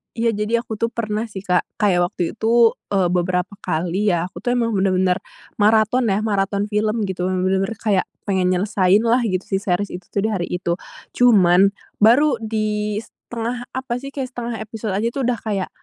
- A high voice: Yes, high, 210 Hz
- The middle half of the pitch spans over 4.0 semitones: No, average, 3.5 semitones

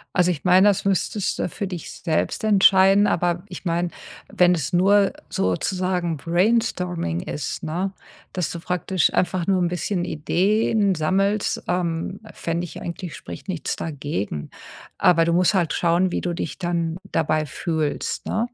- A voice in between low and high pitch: Yes, medium, 180 Hz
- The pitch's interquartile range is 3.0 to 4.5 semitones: No, narrow, 2.4 semitones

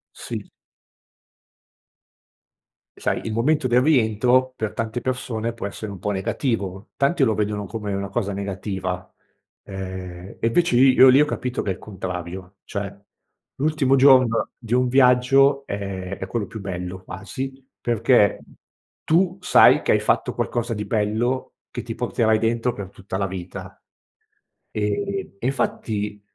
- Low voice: Yes, low, 110 Hz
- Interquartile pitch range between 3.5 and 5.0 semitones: Yes, average, 4.5 semitones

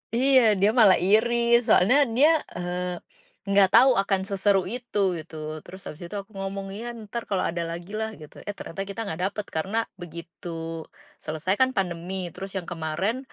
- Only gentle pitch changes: No, average, 3.6 semitones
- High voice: Yes, high, 195 Hz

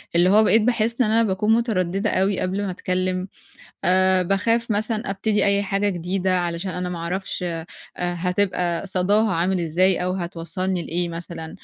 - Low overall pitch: No, medium, 185 Hz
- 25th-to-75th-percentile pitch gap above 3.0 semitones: No, narrow, 2.4 semitones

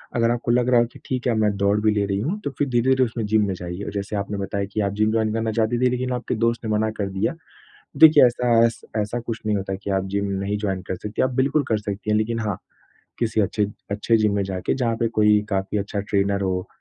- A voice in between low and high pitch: No, low, 110 Hz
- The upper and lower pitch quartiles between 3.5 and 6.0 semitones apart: No, average, 2.8 semitones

